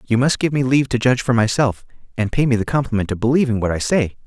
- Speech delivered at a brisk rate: Yes, fast, 265 wpm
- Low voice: Yes, low, 120 Hz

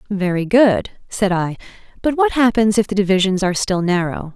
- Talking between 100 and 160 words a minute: No, average, 180 wpm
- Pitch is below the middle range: No, high, 200 Hz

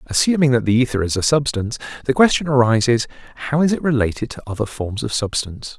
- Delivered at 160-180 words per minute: No, average, 195 wpm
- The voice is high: No, low, 125 Hz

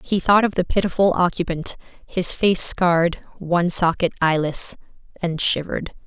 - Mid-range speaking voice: Yes, medium, 175 Hz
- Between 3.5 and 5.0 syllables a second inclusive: Yes, 4.9 syllables/s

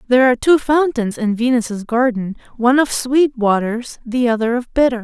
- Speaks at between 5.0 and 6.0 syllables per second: Yes, 5.3 syllables/s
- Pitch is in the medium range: No, high, 245 Hz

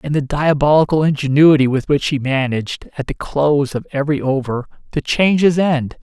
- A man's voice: Yes, male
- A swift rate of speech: No, average, 180 wpm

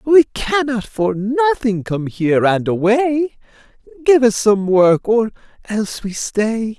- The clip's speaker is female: No, male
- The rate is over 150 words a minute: No, average, 140 wpm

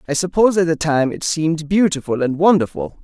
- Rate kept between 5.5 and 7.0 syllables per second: Yes, 6.0 syllables/s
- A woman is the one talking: No, male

